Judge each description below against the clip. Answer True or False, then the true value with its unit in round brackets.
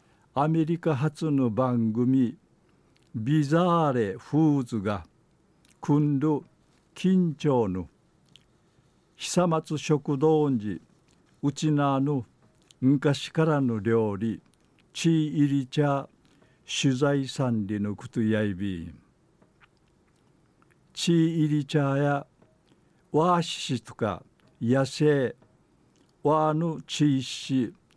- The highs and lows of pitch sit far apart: False (3.8 semitones)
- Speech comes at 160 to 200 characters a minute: True (165 characters per minute)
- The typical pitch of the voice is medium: True (145 Hz)